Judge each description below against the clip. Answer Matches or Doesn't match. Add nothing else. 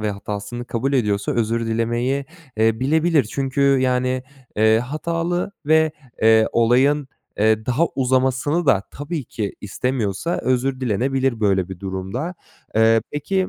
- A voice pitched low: Matches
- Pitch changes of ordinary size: Matches